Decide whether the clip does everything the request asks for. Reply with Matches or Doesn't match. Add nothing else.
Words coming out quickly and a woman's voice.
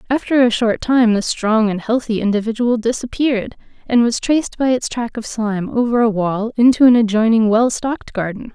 Doesn't match